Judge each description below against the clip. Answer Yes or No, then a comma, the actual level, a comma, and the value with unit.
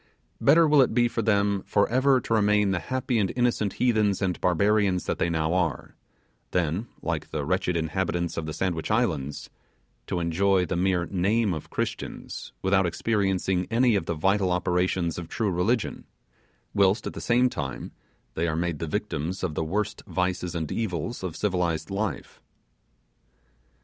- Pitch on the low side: Yes, very low, 95 Hz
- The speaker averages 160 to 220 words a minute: Yes, average, 165 wpm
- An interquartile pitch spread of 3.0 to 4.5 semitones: Yes, average, 3.8 semitones